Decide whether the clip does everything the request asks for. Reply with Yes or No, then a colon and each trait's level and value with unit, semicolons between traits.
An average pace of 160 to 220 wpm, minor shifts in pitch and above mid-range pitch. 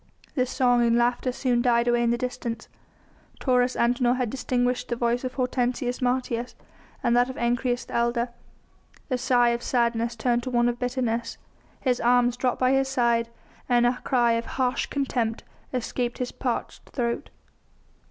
Yes: average, 165 wpm; narrow, 1.0 semitones; high, 245 Hz